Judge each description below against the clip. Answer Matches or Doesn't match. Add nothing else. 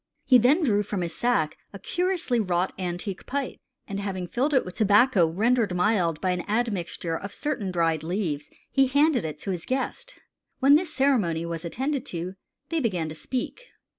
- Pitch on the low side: Doesn't match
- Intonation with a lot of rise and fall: Matches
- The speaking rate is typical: Matches